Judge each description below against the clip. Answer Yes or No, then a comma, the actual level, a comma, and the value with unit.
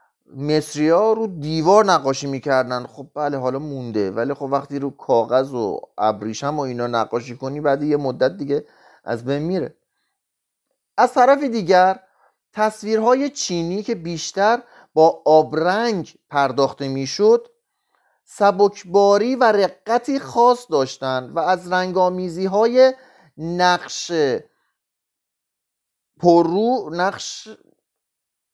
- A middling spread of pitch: No, wide, 7.9 semitones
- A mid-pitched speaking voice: Yes, medium, 175 Hz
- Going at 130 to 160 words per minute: No, slow, 105 wpm